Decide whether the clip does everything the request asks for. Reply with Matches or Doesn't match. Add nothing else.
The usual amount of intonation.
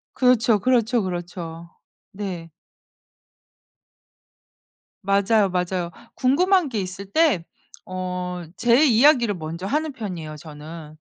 Doesn't match